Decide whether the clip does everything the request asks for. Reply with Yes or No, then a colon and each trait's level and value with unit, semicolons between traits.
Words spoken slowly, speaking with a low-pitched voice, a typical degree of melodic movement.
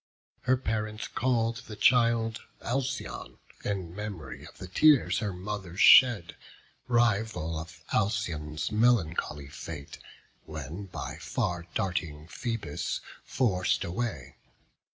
No: slow, 105 wpm; low, 100 Hz; wide, 5.8 semitones